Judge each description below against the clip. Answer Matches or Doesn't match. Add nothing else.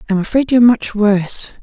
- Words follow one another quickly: Doesn't match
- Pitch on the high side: Matches